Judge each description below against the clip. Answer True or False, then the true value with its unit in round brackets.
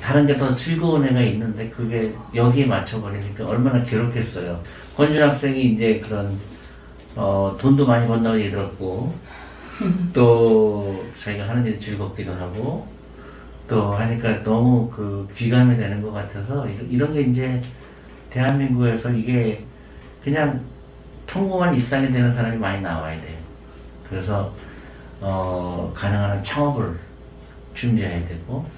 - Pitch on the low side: True (110 Hz)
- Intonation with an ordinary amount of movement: True (4.0 semitones)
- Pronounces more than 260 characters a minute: True (270 characters per minute)